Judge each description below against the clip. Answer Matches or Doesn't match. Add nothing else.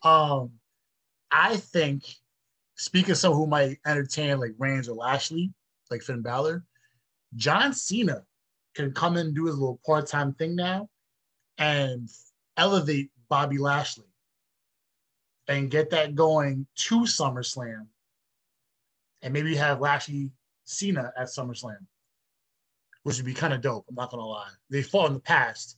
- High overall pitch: Doesn't match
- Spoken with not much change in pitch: Doesn't match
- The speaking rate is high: Doesn't match